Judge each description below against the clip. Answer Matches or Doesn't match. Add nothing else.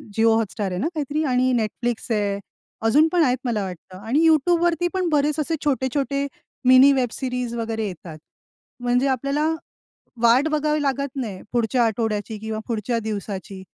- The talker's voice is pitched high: Matches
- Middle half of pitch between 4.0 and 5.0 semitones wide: Matches